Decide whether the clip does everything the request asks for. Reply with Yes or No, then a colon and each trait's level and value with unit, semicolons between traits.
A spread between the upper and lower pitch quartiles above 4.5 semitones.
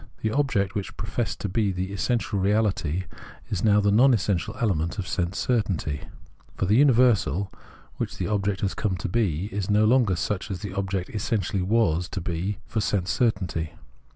No: average, 2.9 semitones